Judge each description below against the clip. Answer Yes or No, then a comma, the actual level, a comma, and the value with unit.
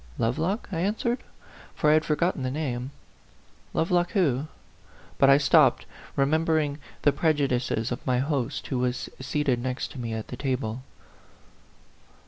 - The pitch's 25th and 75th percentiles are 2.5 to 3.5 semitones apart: No, average, 4.0 semitones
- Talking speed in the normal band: Yes, average, 145 wpm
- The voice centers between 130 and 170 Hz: Yes, medium, 140 Hz